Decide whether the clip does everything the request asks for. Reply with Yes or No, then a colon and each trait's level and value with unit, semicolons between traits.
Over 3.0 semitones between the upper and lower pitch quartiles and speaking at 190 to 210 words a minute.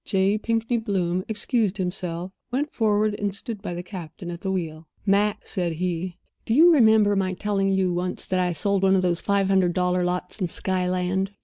No: narrow, 2.5 semitones; average, 195 wpm